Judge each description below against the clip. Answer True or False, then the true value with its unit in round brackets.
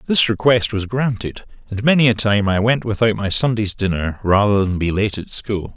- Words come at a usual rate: False (210 wpm)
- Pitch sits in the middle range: False (105 Hz)